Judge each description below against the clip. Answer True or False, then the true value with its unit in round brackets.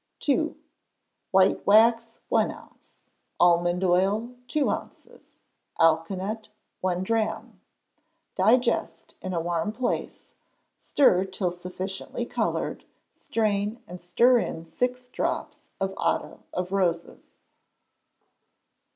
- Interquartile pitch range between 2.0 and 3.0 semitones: False (4.3 semitones)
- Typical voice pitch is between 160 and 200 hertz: True (190 Hz)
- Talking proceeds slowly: True (100 wpm)